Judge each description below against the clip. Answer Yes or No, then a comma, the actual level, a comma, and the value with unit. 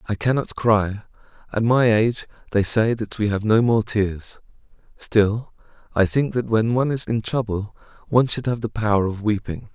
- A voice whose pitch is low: Yes, low, 110 Hz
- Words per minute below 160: No, average, 180 wpm